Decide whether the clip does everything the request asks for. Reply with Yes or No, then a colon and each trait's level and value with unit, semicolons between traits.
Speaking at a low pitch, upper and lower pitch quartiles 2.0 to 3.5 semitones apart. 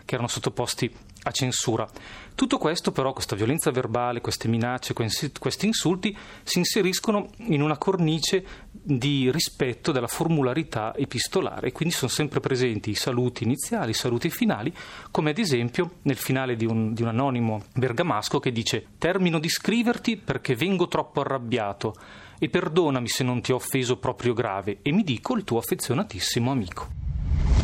No: low, 130 Hz; wide, 5.4 semitones